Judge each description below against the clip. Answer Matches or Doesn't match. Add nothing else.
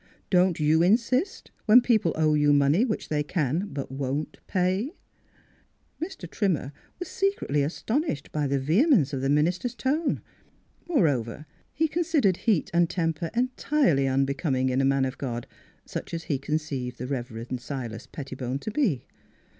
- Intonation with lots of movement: Matches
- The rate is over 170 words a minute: Doesn't match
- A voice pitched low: Doesn't match